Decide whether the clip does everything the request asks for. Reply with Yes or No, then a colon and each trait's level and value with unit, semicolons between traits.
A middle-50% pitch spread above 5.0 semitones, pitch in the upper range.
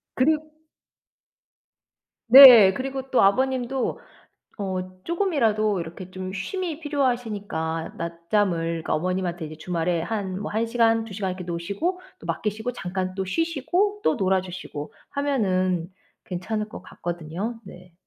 Yes: wide, 5.6 semitones; high, 200 Hz